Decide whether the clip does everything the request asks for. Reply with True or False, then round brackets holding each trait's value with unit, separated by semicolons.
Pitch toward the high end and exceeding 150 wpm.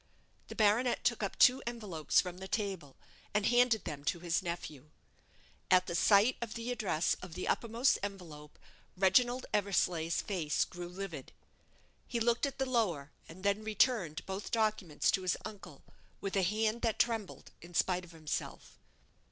True (195 Hz; 160 wpm)